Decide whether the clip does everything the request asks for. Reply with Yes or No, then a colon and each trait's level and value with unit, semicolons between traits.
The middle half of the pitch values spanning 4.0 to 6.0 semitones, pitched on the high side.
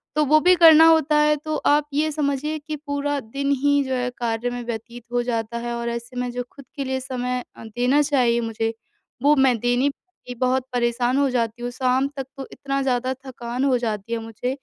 No: average, 3.0 semitones; very high, 255 Hz